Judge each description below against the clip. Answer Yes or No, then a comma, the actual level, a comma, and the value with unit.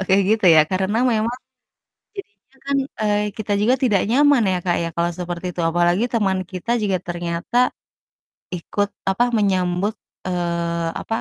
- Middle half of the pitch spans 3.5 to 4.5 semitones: Yes, average, 3.9 semitones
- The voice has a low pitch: No, high, 190 Hz